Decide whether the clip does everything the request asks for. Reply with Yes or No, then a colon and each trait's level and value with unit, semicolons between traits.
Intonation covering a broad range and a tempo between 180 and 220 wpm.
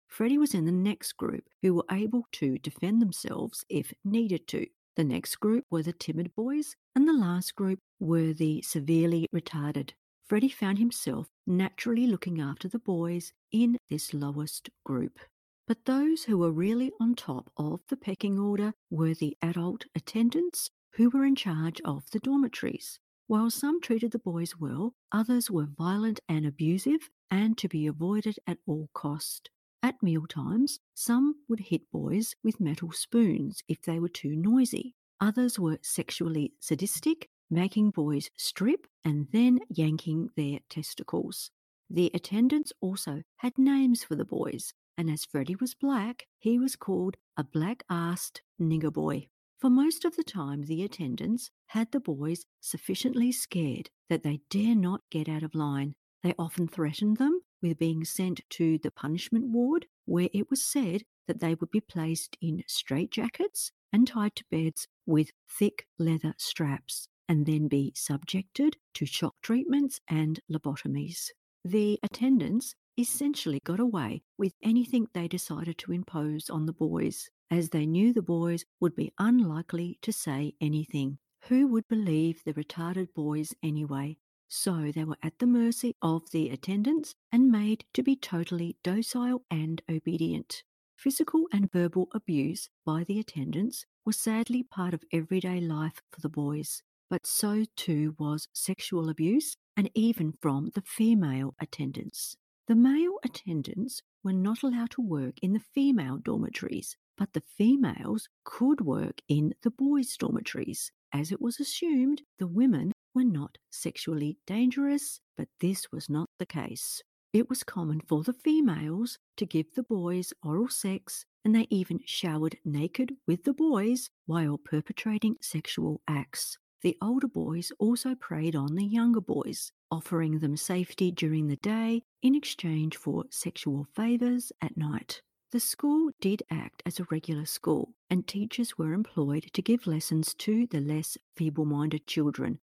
No: wide, 6.8 semitones; average, 155 wpm